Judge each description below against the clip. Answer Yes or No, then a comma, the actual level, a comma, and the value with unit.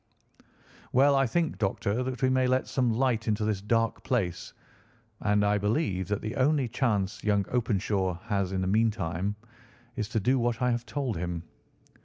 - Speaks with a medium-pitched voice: No, low, 110 Hz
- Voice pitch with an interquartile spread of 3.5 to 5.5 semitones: Yes, average, 4.1 semitones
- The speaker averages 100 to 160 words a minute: No, average, 175 wpm